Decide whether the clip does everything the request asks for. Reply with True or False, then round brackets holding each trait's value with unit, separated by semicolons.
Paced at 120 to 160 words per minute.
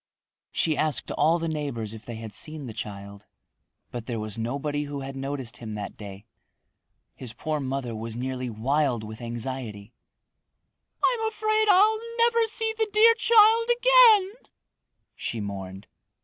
True (150 wpm)